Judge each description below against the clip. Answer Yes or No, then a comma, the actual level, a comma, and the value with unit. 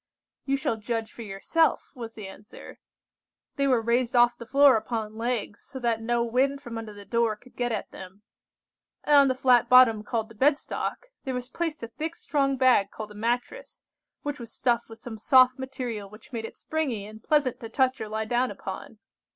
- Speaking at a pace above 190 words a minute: Yes, fast, 205 wpm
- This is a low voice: No, high, 240 Hz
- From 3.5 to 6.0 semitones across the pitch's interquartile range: No, average, 3.1 semitones